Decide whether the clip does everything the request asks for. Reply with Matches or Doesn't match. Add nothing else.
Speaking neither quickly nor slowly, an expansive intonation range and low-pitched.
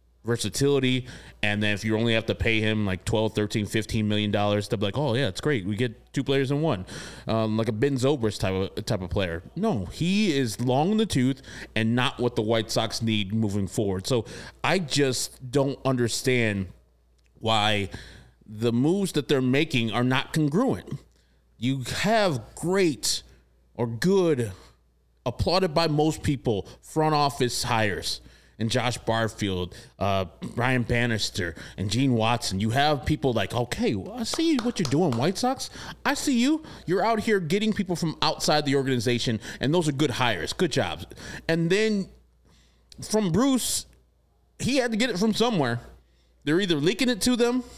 Matches